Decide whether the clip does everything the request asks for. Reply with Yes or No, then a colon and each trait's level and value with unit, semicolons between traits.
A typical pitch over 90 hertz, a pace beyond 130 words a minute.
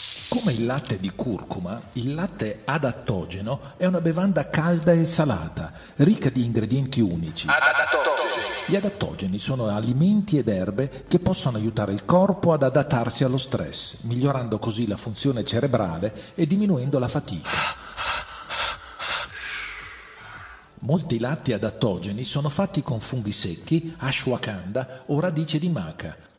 No: low, 135 Hz; average, 125 wpm